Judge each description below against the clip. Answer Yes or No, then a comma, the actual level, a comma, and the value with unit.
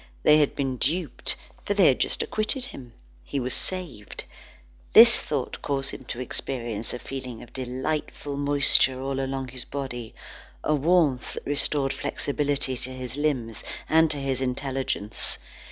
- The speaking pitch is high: No, low, 135 Hz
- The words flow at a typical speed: Yes, average, 155 wpm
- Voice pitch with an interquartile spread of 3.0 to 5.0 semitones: No, narrow, 2.4 semitones